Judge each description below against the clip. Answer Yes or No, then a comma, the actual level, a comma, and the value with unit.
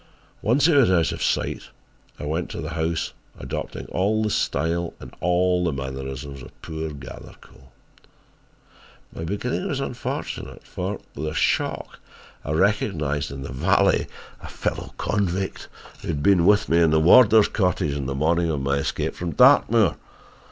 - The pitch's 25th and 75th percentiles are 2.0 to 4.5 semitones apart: No, wide, 5.4 semitones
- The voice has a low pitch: Yes, very low, 85 Hz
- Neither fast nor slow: Yes, average, 160 wpm